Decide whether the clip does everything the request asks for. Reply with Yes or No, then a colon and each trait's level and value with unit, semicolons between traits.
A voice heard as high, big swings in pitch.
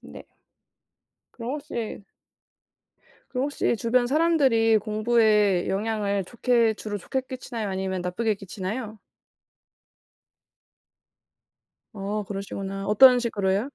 No: high, 215 Hz; average, 3.3 semitones